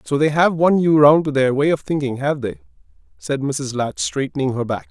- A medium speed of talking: No, fast, 230 wpm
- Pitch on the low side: No, medium, 145 Hz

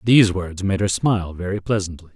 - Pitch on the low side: Yes, very low, 95 Hz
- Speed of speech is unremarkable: Yes, average, 195 wpm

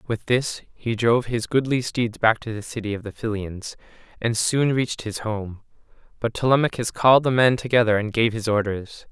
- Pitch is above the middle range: No, low, 115 Hz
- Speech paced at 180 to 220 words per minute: Yes, average, 190 wpm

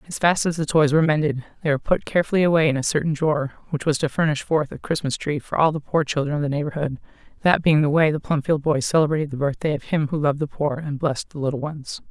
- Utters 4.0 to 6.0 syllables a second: No, 6.8 syllables/s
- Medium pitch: Yes, medium, 150 Hz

